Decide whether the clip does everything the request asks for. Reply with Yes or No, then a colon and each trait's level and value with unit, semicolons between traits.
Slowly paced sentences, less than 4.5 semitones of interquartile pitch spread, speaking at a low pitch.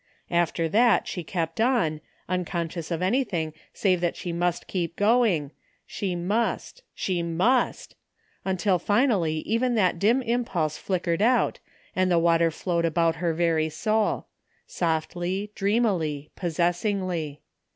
No: slow, 130 wpm; average, 3.7 semitones; medium, 175 Hz